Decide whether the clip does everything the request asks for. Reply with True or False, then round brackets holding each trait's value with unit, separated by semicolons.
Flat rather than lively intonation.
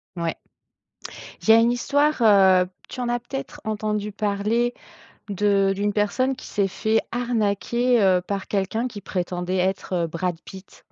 False (3.8 semitones)